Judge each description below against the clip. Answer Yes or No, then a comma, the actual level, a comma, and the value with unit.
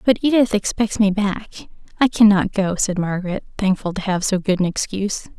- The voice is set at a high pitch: Yes, high, 200 Hz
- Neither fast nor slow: Yes, average, 180 wpm